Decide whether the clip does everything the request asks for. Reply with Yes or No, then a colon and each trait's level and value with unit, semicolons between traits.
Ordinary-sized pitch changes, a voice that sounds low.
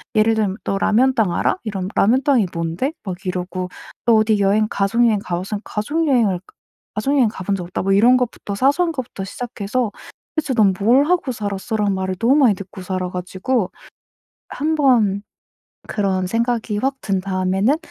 No: average, 4.6 semitones; high, 210 Hz